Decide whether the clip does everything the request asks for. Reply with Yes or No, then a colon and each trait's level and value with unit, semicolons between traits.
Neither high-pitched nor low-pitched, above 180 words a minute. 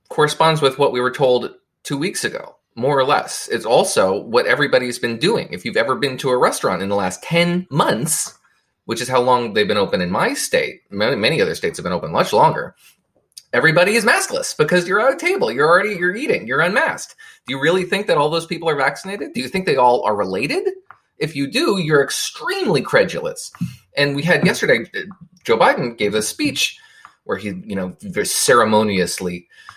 Yes: medium, 165 Hz; average, 200 wpm